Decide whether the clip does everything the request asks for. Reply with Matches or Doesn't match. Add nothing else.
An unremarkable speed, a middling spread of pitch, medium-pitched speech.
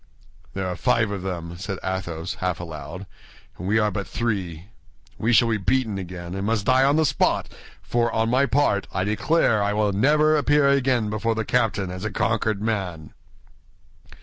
Doesn't match